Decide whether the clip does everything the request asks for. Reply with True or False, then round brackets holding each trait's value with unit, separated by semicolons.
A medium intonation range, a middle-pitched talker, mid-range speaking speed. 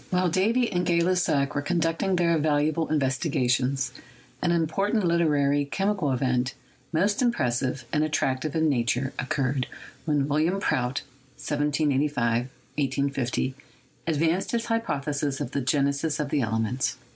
False (4.2 semitones; 145 Hz; 130 wpm)